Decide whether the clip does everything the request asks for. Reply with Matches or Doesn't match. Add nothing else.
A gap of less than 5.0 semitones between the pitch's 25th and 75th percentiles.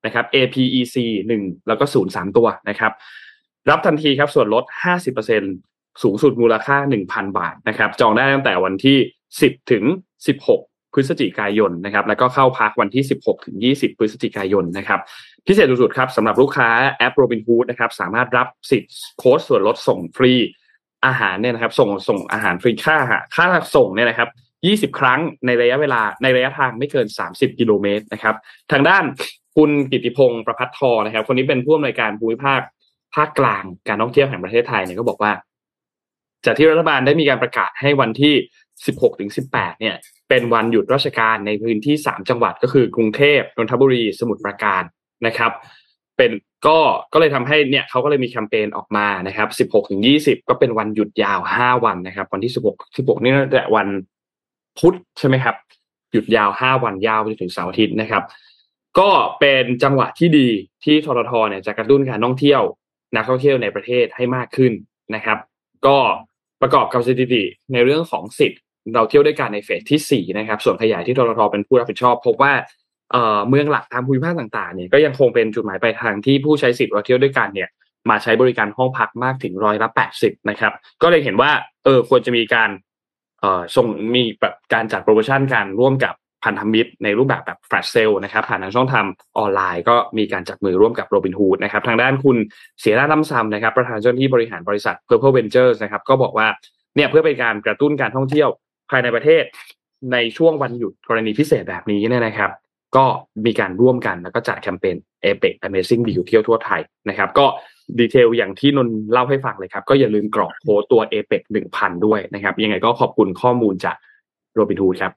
Matches